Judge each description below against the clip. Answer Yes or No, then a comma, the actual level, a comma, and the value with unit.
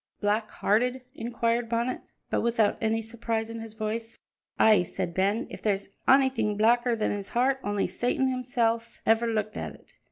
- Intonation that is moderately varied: No, narrow, 1.9 semitones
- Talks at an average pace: Yes, average, 165 wpm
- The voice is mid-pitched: No, high, 225 Hz